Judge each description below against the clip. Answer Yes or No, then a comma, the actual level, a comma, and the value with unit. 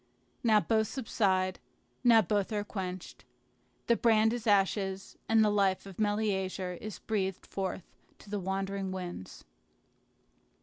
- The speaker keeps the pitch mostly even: Yes, narrow, 2.3 semitones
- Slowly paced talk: Yes, slow, 130 wpm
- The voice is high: Yes, high, 200 Hz